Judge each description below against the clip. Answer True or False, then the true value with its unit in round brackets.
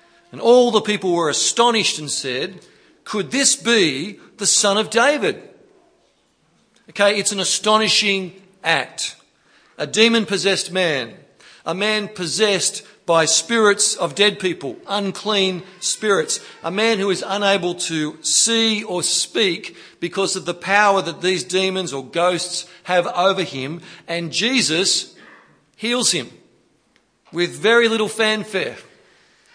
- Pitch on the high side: True (195 Hz)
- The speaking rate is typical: False (130 wpm)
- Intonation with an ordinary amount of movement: True (3.4 semitones)